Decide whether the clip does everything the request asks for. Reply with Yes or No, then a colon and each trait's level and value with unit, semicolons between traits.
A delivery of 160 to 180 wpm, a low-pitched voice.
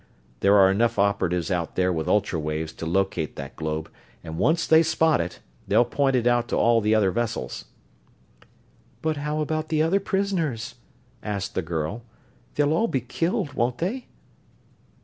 Yes: average, 170 wpm; low, 115 Hz